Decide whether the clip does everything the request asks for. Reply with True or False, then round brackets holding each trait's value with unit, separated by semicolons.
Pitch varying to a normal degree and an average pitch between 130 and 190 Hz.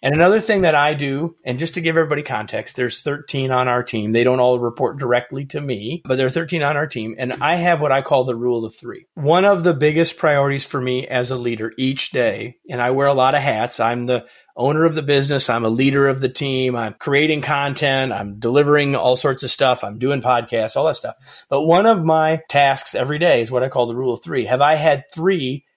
True (3.5 semitones; 135 Hz)